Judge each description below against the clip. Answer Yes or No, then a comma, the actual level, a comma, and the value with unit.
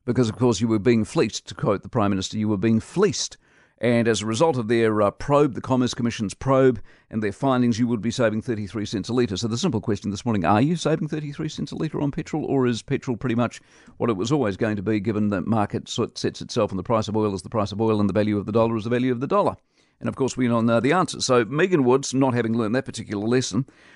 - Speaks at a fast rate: Yes, fast, 285 wpm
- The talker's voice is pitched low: Yes, low, 115 Hz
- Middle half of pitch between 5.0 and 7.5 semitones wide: No, average, 2.9 semitones